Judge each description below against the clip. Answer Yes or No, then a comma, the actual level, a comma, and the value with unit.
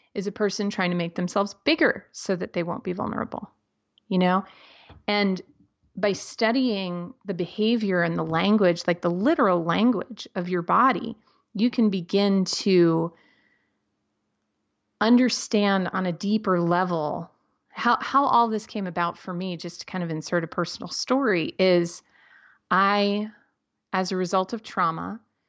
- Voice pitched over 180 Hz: Yes, high, 190 Hz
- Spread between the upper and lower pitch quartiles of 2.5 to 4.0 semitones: Yes, average, 3.2 semitones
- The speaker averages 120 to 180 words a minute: Yes, average, 150 wpm